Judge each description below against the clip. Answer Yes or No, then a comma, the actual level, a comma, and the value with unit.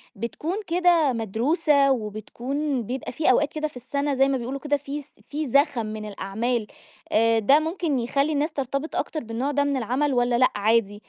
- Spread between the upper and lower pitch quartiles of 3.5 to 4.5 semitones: Yes, average, 4.1 semitones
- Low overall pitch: No, very high, 270 Hz